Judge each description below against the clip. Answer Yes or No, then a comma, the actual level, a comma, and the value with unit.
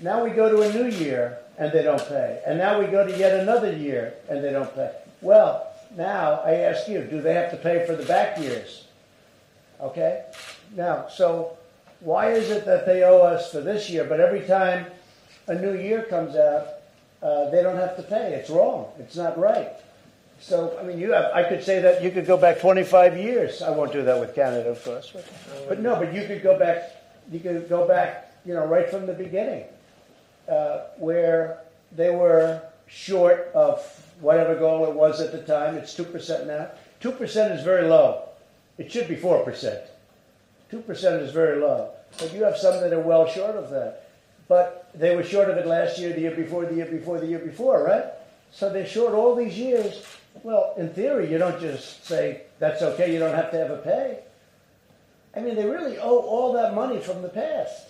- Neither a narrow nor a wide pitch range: Yes, average, 4.6 semitones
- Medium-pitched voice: Yes, medium, 180 Hz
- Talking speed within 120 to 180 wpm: No, fast, 205 wpm